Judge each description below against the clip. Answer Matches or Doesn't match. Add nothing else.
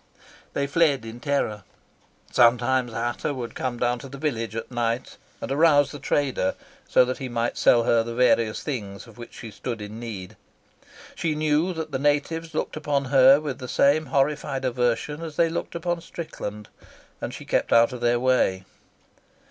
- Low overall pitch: Matches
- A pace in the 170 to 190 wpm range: Matches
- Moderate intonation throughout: Matches